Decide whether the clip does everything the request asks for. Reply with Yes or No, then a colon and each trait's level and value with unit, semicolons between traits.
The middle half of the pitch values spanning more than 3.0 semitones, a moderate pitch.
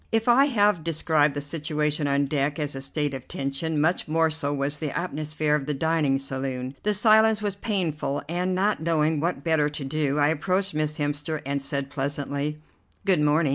No: average, 2.7 semitones; medium, 150 Hz